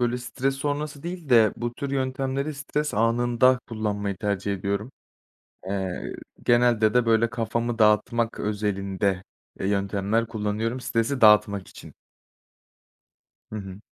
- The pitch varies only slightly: No, average, 3.5 semitones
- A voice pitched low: Yes, low, 115 Hz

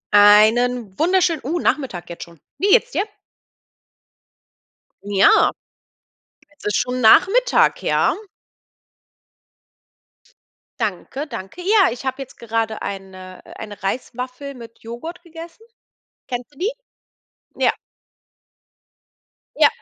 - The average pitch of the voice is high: Yes, very high, 250 Hz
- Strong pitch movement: Yes, wide, 7.9 semitones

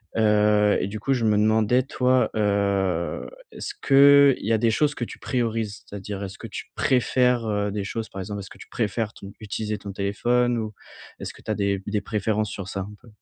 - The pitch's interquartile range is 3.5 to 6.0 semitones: No, average, 2.8 semitones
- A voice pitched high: No, low, 105 Hz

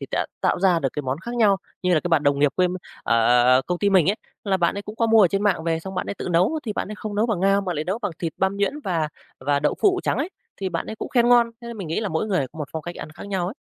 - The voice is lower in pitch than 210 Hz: Yes, high, 190 Hz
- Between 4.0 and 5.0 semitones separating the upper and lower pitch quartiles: Yes, average, 4.4 semitones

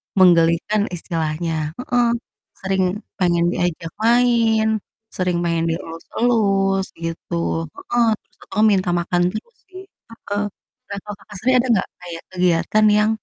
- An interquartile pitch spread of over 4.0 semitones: Yes, average, 4.4 semitones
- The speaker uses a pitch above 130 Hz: Yes, high, 190 Hz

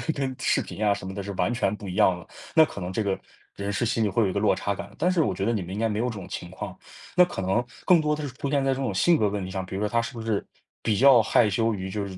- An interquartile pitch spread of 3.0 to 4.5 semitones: Yes, average, 4.1 semitones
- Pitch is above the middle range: No, low, 105 Hz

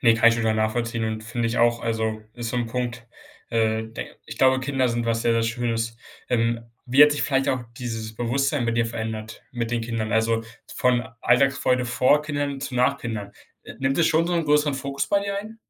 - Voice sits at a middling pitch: No, low, 120 Hz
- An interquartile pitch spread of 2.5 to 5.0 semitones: Yes, average, 2.9 semitones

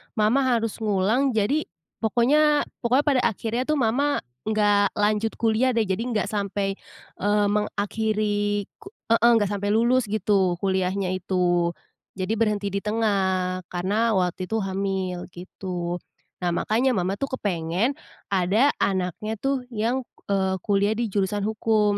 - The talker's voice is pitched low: No, high, 205 Hz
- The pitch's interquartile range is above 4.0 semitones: No, average, 3.0 semitones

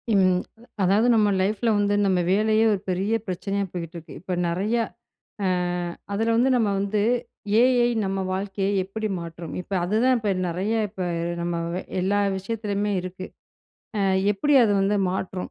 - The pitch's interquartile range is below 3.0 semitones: Yes, narrow, 2.6 semitones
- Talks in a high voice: Yes, high, 195 Hz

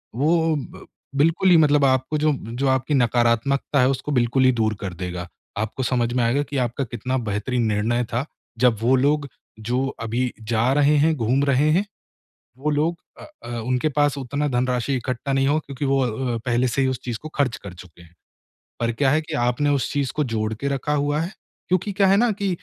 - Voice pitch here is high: No, low, 130 Hz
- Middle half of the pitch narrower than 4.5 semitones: Yes, average, 3.5 semitones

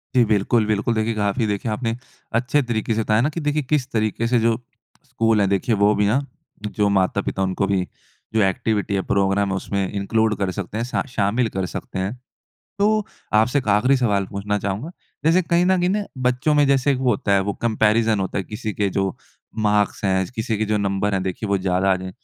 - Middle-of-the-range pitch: No, low, 105 Hz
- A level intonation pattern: No, average, 3.4 semitones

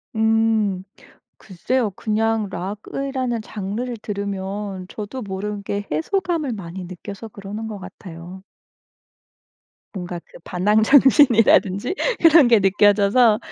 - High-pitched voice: Yes, high, 210 Hz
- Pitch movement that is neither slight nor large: Yes, average, 3.0 semitones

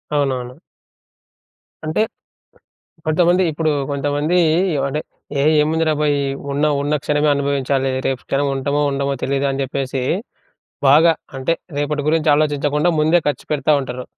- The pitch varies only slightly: Yes, narrow, 1.9 semitones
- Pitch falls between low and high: Yes, medium, 145 Hz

